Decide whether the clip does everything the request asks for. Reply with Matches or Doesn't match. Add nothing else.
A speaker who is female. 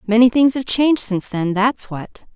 Matches